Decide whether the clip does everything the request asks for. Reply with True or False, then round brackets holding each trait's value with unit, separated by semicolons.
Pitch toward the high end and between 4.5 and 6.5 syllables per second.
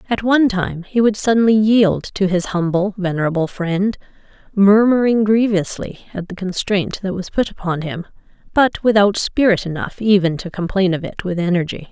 True (195 Hz; 5.1 syllables/s)